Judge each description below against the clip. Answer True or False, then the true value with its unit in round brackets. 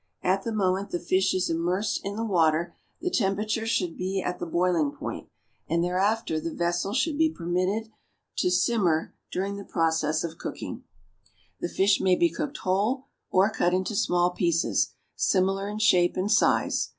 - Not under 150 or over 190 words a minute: True (170 wpm)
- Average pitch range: True (3.0 semitones)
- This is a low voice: False (185 Hz)